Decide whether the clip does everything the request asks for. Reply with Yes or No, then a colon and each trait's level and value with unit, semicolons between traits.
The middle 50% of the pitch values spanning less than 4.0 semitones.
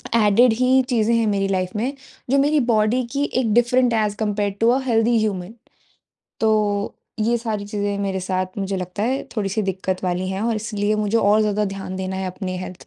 Yes: average, 3.1 semitones